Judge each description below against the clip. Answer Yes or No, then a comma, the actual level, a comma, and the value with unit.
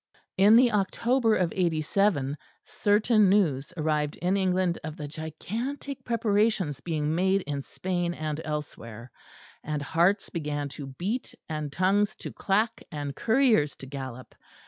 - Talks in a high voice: No, medium, 175 Hz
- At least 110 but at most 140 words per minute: Yes, slow, 135 wpm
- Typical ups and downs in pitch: No, wide, 5.8 semitones